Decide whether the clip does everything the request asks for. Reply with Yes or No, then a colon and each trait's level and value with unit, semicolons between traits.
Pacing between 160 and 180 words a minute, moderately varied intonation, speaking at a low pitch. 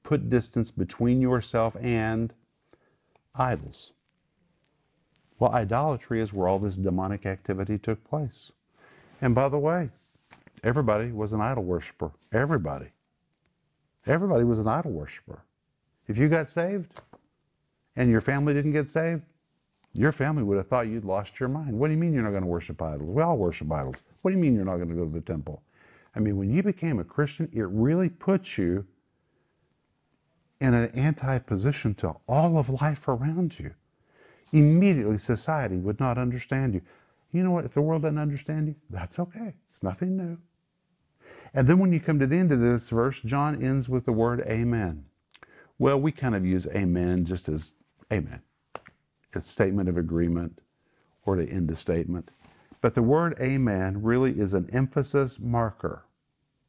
No: average, 170 wpm; wide, 7.2 semitones; low, 125 Hz